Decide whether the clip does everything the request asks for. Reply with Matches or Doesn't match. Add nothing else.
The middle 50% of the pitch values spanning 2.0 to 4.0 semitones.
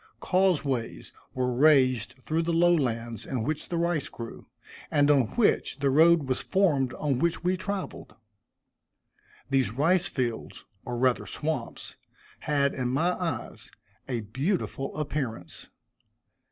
Doesn't match